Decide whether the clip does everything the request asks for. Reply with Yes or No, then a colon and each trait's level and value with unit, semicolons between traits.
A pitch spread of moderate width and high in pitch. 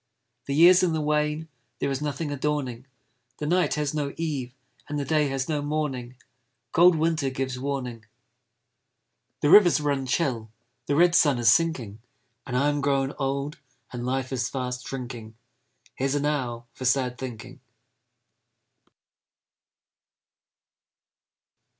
No: average, 3.0 semitones; medium, 140 Hz